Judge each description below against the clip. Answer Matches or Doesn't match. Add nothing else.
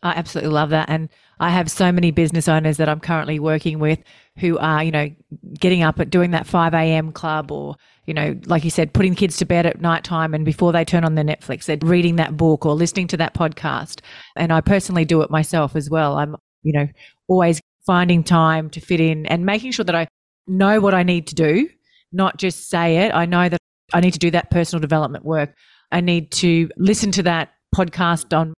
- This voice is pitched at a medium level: Matches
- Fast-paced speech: Matches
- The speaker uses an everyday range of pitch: Doesn't match